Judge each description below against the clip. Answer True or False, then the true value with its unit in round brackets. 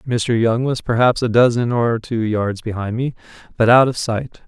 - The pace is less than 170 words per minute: False (200 wpm)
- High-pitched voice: False (115 Hz)